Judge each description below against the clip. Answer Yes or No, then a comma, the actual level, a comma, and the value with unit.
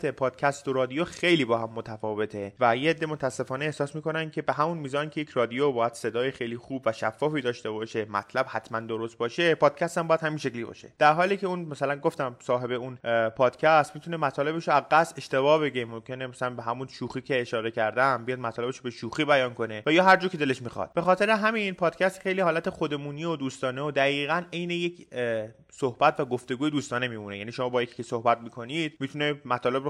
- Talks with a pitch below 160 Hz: Yes, low, 135 Hz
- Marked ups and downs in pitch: No, average, 4.5 semitones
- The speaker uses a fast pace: Yes, fast, 200 wpm